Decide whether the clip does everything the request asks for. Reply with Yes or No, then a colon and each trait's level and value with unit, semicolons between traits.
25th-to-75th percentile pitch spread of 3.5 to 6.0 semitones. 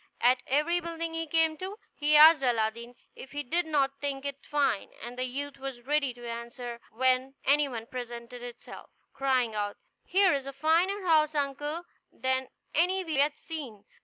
Yes: average, 4.2 semitones